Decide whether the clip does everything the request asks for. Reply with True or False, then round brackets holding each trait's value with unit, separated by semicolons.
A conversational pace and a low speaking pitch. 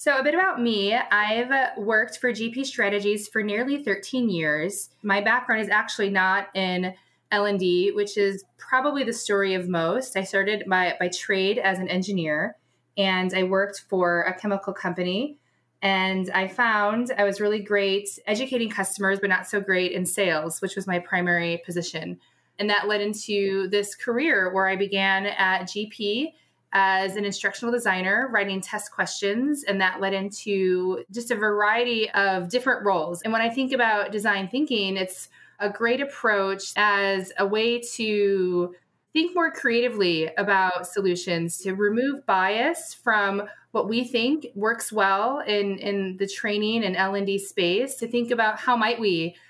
False (165 wpm; 200 Hz)